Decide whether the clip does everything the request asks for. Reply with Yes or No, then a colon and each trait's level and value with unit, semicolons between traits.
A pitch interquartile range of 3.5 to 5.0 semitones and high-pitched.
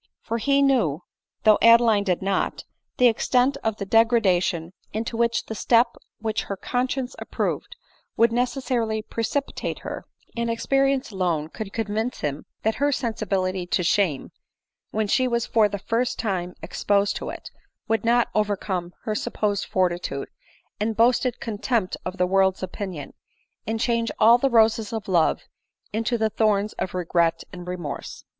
Yes: average, 3.8 semitones; high, 220 Hz